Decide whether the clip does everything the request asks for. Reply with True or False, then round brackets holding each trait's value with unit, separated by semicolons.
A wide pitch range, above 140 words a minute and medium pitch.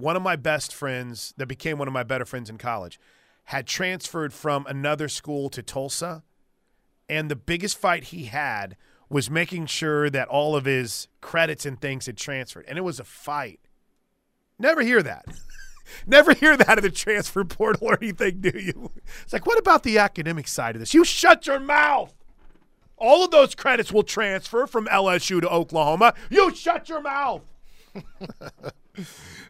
True (7.8 semitones; 175 wpm; 165 Hz)